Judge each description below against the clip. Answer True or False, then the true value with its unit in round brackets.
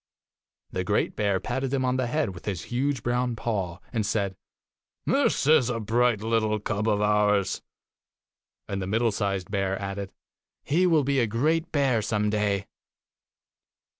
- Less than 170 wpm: True (160 wpm)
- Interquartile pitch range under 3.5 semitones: False (4.0 semitones)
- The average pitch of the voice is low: True (110 Hz)